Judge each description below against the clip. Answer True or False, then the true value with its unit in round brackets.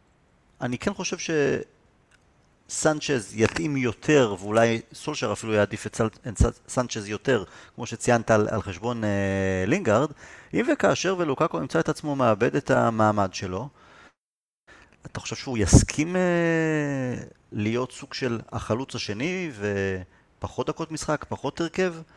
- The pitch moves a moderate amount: False (6.1 semitones)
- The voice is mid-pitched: False (125 Hz)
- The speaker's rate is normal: True (120 wpm)